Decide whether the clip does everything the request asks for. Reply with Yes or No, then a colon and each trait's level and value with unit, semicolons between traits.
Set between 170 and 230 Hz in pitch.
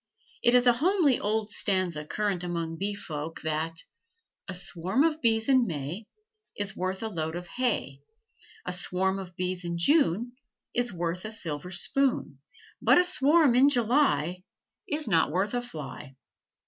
Yes: high, 190 Hz